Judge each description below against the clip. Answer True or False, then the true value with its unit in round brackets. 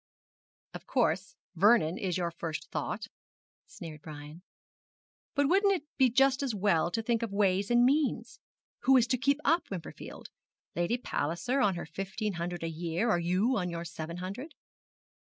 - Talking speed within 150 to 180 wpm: True (165 wpm)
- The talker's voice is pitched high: True (195 Hz)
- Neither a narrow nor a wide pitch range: False (6.6 semitones)